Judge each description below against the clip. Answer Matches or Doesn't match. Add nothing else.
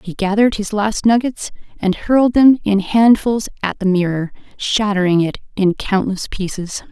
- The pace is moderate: Matches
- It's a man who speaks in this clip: Doesn't match